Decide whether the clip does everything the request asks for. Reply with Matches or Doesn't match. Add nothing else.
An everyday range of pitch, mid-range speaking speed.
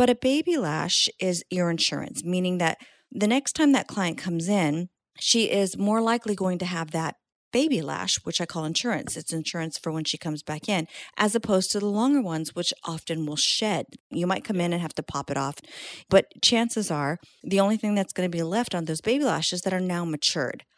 Doesn't match